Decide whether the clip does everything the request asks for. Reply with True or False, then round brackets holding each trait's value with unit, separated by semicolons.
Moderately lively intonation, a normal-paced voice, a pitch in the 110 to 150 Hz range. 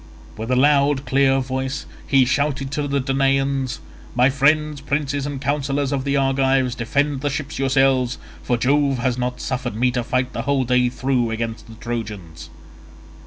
False (1.9 semitones; 165 wpm; 135 Hz)